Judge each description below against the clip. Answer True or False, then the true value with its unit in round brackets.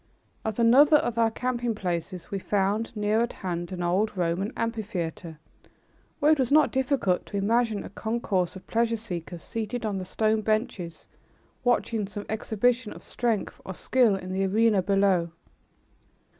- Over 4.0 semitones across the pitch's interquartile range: False (3.5 semitones)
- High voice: True (210 Hz)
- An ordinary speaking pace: True (155 wpm)